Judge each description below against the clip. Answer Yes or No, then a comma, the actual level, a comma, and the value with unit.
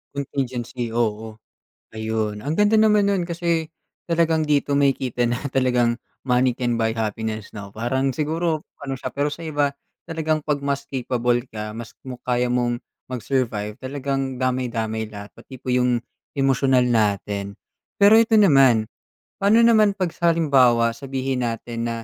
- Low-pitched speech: Yes, low, 130 Hz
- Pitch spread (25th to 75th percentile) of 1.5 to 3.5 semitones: No, average, 4.0 semitones